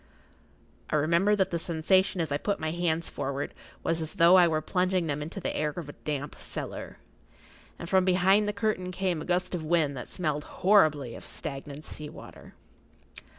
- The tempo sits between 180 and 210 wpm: Yes, average, 190 wpm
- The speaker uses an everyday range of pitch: Yes, average, 3.5 semitones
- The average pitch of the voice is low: No, medium, 170 Hz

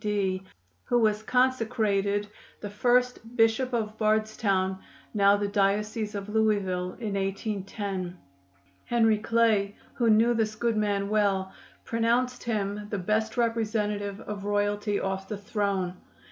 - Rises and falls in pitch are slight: Yes, narrow, 2.1 semitones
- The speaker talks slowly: Yes, slow, 125 wpm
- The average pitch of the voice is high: Yes, high, 210 Hz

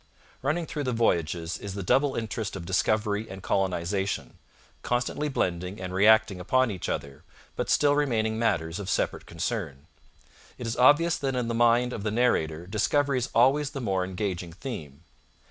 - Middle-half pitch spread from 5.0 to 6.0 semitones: Yes, wide, 5.4 semitones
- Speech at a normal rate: Yes, average, 165 wpm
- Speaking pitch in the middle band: No, low, 110 Hz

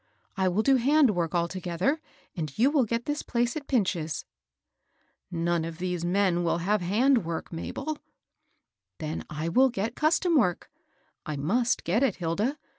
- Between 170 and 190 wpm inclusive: Yes, average, 175 wpm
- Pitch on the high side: Yes, high, 195 Hz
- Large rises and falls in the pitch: Yes, wide, 6.8 semitones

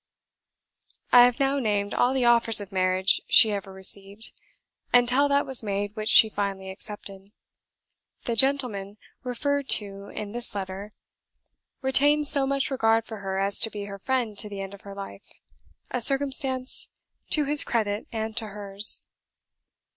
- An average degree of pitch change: Yes, average, 4.4 semitones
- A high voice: Yes, high, 215 Hz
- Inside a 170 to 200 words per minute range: No, average, 160 wpm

